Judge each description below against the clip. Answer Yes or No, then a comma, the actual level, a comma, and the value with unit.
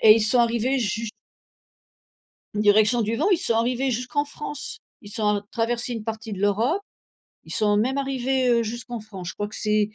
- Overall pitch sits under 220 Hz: No, high, 230 Hz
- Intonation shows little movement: No, average, 3.0 semitones